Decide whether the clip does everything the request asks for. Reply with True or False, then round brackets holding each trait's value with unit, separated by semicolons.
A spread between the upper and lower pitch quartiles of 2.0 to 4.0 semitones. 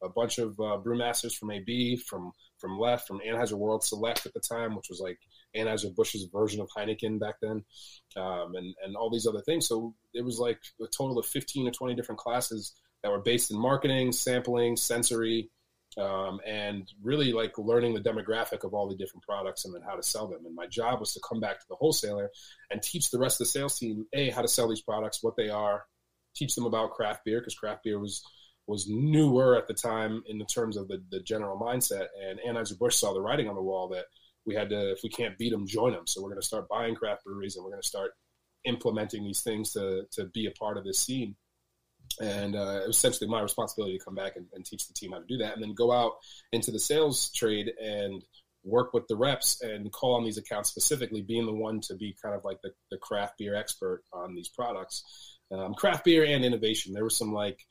True (2.7 semitones)